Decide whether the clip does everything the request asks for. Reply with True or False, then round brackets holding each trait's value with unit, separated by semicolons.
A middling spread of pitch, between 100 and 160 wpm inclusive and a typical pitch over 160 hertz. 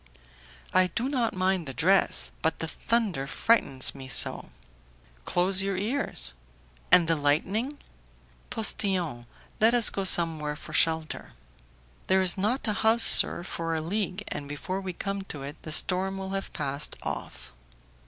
True (4.3 semitones; 155 wpm; 185 Hz)